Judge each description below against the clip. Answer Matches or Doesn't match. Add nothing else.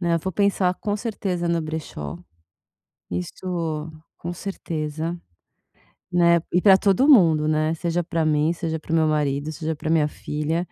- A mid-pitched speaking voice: Matches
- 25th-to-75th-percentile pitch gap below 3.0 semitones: Matches